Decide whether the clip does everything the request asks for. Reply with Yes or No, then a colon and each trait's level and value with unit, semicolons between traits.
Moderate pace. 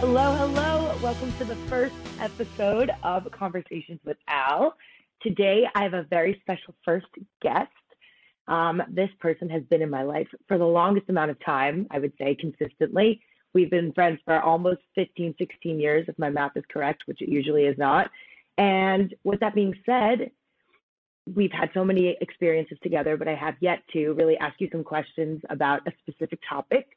Yes: average, 180 wpm